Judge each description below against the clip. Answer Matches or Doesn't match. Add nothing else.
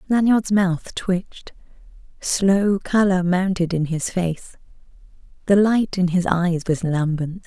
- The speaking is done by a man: Doesn't match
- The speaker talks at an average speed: Doesn't match